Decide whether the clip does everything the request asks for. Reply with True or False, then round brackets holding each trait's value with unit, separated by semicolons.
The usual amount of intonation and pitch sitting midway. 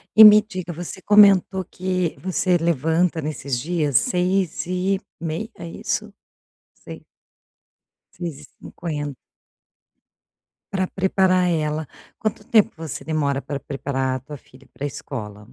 True (4.3 semitones; 170 Hz)